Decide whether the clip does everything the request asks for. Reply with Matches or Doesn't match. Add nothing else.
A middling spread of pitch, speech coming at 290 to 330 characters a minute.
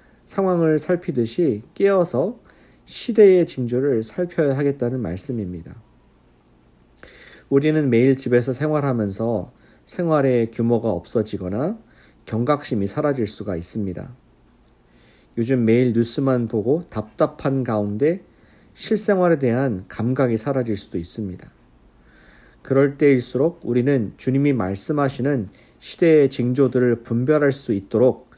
Doesn't match